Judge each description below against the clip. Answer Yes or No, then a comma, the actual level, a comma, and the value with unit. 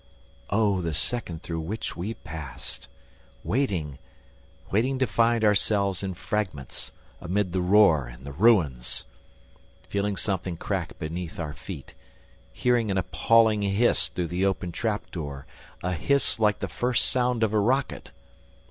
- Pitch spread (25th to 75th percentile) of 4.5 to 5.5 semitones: Yes, average, 5.0 semitones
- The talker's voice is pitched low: Yes, low, 100 Hz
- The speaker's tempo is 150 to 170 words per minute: No, average, 140 wpm